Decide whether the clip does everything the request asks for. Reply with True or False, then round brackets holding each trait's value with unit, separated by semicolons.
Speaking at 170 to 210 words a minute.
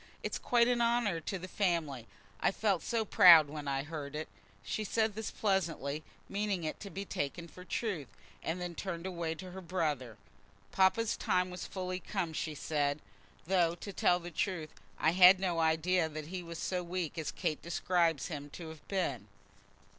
True (185 wpm)